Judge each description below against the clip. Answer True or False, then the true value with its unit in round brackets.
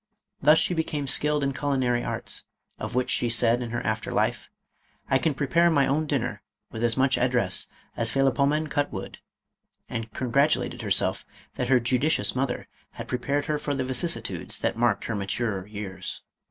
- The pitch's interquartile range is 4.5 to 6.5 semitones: False (3.5 semitones)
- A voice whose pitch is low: True (130 Hz)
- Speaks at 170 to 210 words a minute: True (180 wpm)